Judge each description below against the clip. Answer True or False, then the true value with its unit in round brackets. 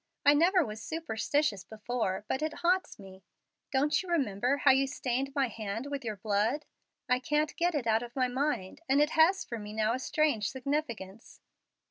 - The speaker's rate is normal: True (185 wpm)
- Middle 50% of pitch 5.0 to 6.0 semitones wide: True (5.4 semitones)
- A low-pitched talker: False (260 Hz)